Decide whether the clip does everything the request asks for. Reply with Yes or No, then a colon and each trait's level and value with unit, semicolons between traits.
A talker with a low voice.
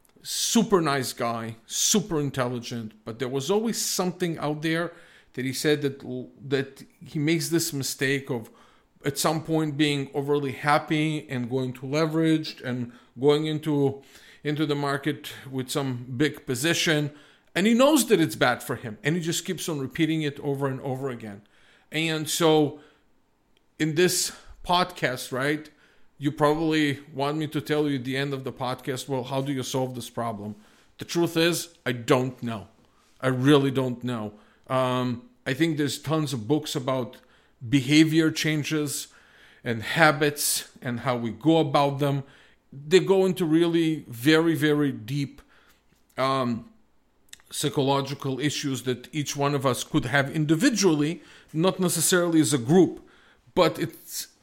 No: medium, 145 Hz